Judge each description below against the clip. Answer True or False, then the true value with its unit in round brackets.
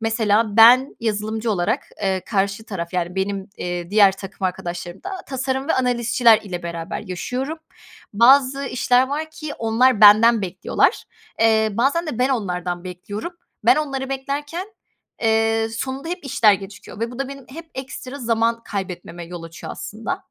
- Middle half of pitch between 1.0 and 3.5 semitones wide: False (5.2 semitones)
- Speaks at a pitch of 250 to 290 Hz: False (225 Hz)